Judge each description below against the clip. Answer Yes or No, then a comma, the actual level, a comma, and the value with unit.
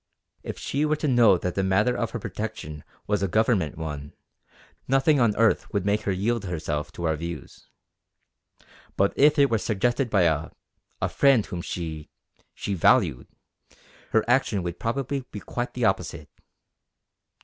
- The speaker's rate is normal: Yes, average, 160 wpm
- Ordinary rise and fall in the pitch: No, wide, 6.0 semitones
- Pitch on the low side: Yes, low, 105 Hz